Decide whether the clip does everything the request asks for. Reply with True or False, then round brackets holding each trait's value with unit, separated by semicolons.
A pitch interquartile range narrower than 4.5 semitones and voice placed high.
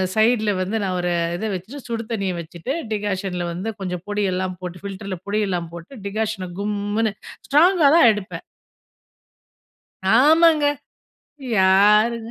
True (3.3 semitones; 205 Hz)